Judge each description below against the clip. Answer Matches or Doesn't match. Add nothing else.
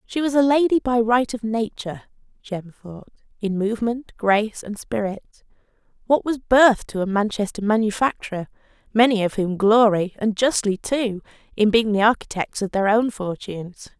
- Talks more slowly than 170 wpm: Matches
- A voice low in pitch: Doesn't match